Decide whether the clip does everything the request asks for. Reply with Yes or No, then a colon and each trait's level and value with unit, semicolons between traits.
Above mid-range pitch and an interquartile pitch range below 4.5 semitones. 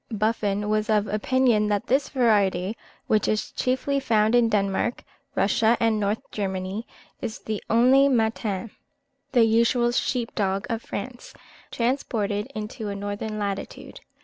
Yes: high, 215 Hz; narrow, 2.6 semitones